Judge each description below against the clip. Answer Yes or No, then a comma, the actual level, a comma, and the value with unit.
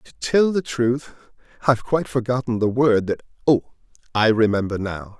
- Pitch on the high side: No, low, 120 Hz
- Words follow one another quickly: No, average, 150 wpm